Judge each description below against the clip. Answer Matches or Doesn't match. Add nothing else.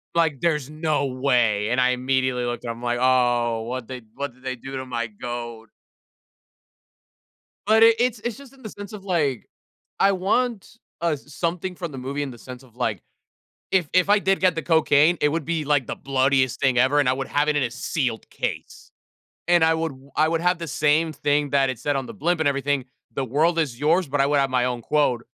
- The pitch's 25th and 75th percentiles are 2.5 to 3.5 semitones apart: Doesn't match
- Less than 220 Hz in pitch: Matches